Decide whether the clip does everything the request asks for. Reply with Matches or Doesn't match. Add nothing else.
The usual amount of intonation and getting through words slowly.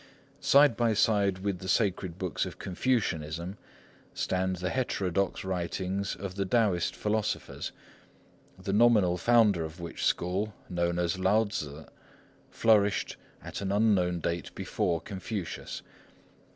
Matches